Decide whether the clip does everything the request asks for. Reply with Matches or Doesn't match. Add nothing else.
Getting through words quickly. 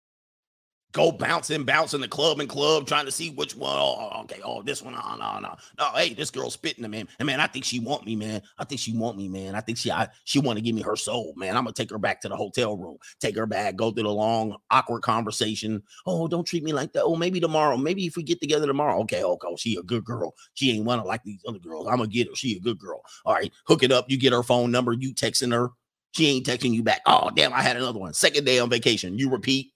Matches